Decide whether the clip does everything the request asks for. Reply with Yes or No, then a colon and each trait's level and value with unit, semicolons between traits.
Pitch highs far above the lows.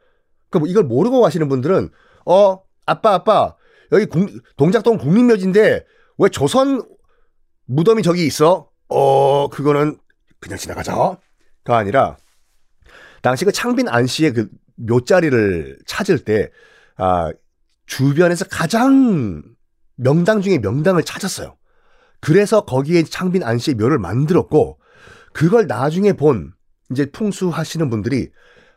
Yes: wide, 7.3 semitones